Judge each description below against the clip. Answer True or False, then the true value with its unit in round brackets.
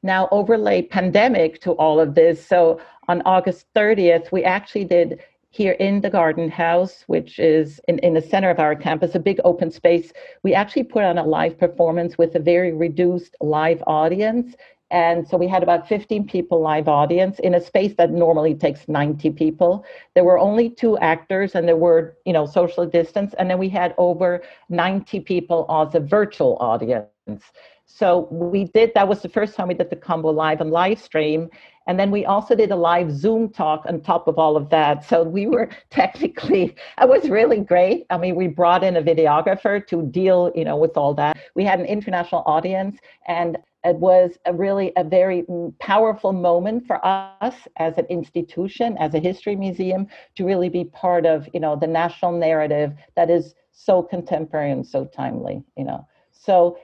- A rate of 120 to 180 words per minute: False (190 wpm)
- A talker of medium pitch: True (175 Hz)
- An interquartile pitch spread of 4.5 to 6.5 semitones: False (2.7 semitones)